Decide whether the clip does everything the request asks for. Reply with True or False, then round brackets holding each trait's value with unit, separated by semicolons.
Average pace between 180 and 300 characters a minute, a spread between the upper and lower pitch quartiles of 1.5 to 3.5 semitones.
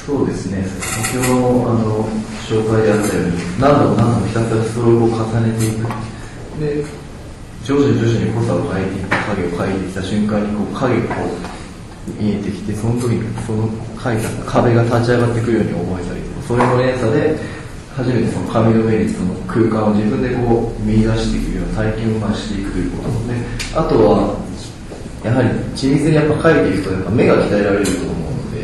False (375 characters per minute; 2.4 semitones)